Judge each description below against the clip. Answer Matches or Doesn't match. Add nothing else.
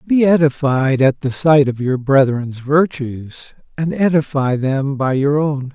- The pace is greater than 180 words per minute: Doesn't match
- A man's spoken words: Matches